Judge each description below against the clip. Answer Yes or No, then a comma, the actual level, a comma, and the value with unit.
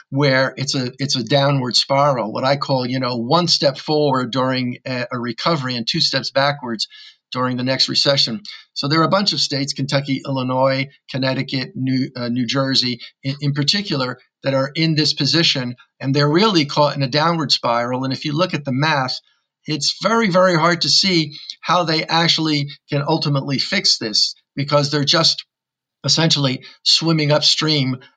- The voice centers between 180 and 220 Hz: No, medium, 140 Hz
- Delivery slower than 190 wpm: Yes, average, 175 wpm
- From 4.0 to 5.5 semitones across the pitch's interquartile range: No, average, 3.0 semitones